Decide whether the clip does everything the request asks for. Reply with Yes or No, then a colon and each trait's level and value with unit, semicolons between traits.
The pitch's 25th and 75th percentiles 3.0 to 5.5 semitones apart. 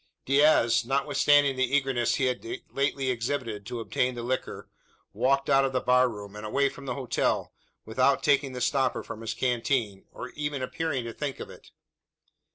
No: narrow, 2.6 semitones